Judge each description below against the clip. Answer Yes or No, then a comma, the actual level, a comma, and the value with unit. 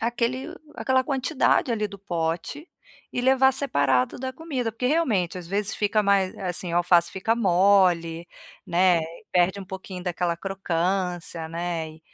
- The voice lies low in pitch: No, high, 190 Hz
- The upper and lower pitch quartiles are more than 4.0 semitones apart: Yes, wide, 5.5 semitones